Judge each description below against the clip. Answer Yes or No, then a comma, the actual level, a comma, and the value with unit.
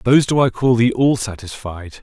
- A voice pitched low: Yes, low, 120 Hz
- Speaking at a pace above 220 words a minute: No, fast, 205 wpm